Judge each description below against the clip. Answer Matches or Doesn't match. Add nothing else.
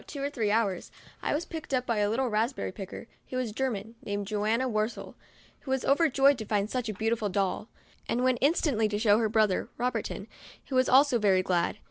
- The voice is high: Matches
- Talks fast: Matches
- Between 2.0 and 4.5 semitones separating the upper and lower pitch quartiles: Matches